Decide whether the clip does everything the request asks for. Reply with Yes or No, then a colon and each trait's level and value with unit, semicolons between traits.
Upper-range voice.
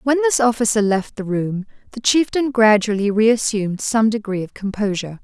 Yes: high, 220 Hz